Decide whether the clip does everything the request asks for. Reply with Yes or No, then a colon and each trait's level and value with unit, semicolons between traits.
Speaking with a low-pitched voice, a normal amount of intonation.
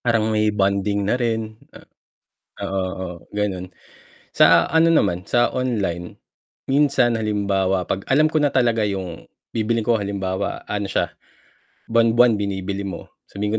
Yes: low, 105 Hz; average, 3.1 semitones